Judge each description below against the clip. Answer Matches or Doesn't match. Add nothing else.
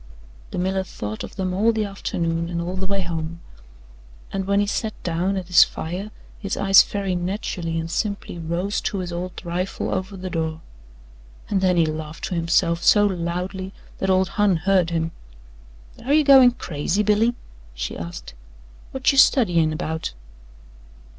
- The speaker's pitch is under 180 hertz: Doesn't match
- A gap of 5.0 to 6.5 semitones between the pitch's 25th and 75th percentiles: Doesn't match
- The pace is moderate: Matches